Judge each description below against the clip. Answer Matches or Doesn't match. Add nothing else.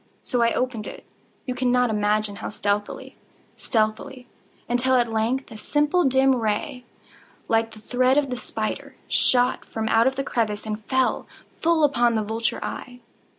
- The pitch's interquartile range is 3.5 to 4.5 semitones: Doesn't match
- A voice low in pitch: Doesn't match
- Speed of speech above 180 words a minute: Doesn't match